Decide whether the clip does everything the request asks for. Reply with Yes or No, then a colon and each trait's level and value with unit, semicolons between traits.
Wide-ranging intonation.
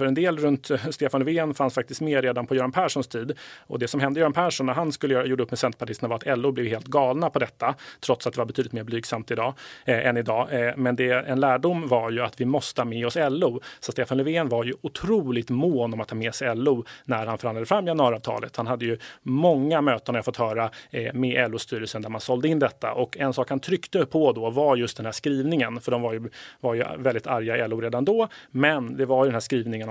No: average, 2.8 semitones